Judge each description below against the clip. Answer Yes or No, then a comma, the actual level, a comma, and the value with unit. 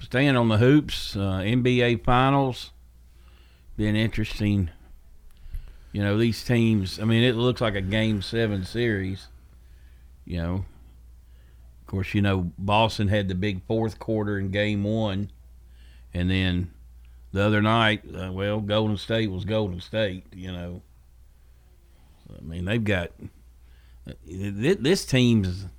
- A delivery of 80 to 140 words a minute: Yes, slow, 135 wpm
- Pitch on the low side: Yes, very low, 95 Hz